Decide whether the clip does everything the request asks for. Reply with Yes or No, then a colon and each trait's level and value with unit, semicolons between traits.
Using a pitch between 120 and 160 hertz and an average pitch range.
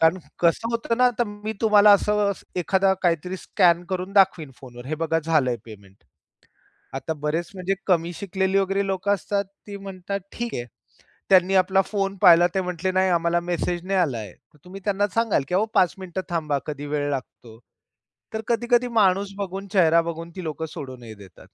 No: medium, 185 Hz; average, 3.4 semitones